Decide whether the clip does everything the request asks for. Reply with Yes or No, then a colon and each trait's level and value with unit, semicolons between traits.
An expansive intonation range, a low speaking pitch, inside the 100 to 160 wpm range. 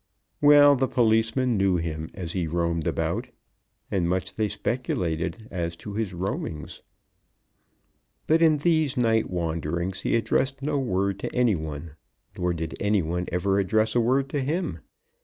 Yes: wide, 6.6 semitones; low, 100 Hz; average, 155 wpm